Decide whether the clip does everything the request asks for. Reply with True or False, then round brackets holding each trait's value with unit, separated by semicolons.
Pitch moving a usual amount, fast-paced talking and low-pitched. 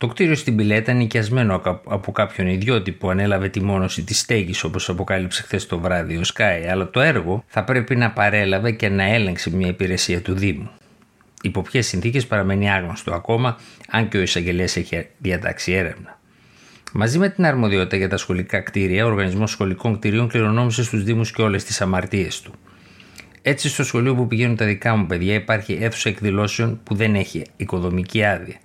True (3.5 semitones; 180 wpm; 100 Hz)